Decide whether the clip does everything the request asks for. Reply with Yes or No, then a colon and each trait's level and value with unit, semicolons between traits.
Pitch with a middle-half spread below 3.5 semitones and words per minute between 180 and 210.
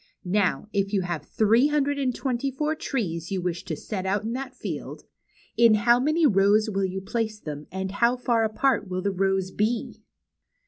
No: average, 4.5 semitones; average, 190 wpm